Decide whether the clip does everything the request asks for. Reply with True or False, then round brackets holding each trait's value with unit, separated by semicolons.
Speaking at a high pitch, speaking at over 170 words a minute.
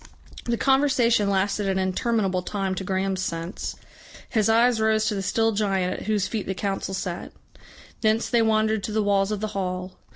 True (205 Hz; 185 wpm)